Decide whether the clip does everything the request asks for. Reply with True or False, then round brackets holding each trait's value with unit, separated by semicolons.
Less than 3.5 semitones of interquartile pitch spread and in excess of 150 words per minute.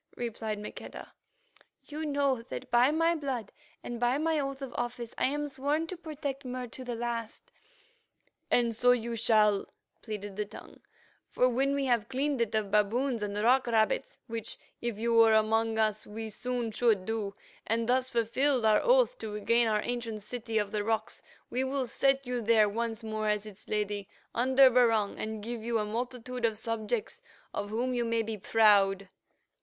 True (2.8 semitones; 180 wpm)